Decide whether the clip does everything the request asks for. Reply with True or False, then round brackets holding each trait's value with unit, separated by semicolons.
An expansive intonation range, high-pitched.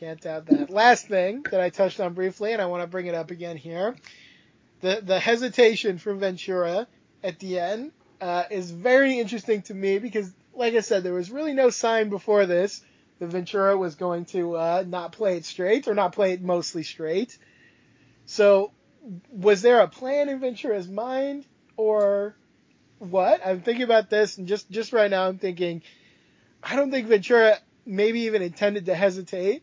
False (3.7 semitones; 200 Hz)